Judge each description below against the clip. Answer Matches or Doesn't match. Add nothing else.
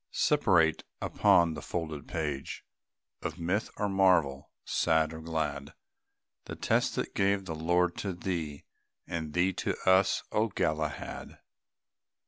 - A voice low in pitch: Matches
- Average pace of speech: Doesn't match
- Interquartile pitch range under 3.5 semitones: Matches